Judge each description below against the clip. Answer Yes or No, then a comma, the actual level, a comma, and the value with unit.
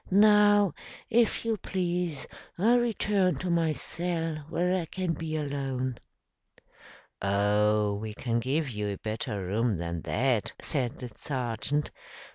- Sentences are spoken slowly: Yes, slow, 130 wpm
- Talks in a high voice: No, medium, 145 Hz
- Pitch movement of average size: No, wide, 8.3 semitones